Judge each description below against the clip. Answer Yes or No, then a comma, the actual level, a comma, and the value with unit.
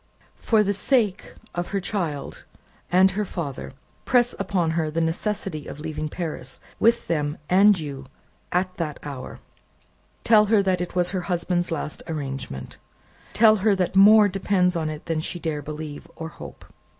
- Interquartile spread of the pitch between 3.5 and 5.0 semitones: Yes, average, 4.3 semitones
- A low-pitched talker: No, medium, 175 Hz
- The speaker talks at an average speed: Yes, average, 160 wpm